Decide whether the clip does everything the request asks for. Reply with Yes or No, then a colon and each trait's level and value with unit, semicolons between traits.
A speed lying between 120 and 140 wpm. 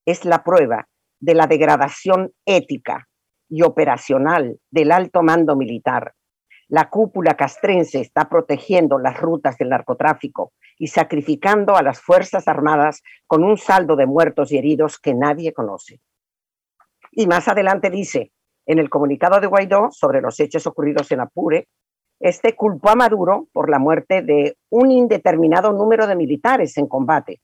No: average, 150 wpm